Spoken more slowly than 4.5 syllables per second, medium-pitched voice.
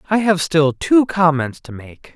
Yes: 4.2 syllables/s; medium, 165 Hz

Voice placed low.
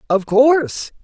No: high, 240 Hz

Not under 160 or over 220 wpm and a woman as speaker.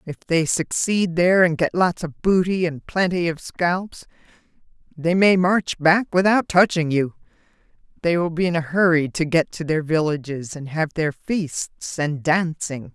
Yes: average, 170 wpm; female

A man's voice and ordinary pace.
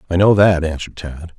No: male; fast, 215 wpm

